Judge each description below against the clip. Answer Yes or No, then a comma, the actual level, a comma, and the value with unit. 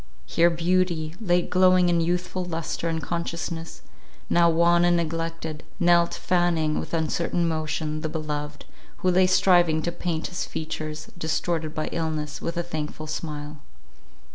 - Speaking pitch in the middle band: Yes, medium, 165 Hz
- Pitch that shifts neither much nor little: No, narrow, 1.8 semitones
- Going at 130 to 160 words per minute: Yes, average, 140 wpm